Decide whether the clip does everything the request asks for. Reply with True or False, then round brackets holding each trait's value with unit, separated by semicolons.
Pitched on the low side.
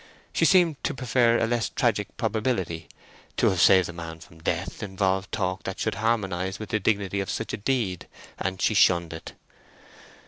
True (100 Hz)